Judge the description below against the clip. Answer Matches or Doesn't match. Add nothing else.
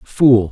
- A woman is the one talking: Doesn't match